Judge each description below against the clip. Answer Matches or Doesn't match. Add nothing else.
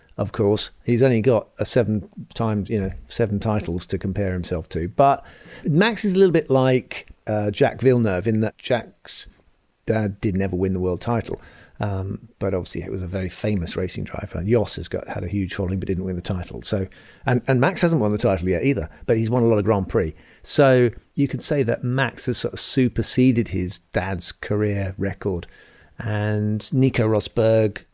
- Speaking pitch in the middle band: Doesn't match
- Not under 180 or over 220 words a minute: Matches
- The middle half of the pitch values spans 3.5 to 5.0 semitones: Matches